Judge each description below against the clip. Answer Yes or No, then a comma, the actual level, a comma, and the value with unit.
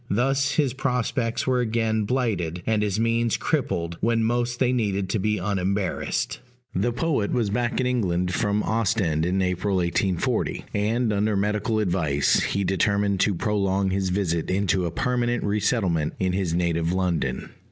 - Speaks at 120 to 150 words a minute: No, average, 160 wpm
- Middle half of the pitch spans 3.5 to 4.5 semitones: Yes, average, 4.2 semitones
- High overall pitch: No, low, 105 Hz